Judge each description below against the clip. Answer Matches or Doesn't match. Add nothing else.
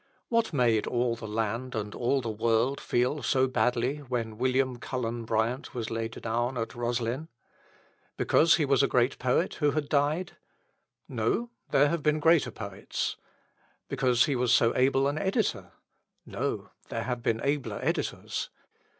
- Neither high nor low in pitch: Doesn't match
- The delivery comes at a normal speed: Matches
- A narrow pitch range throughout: Doesn't match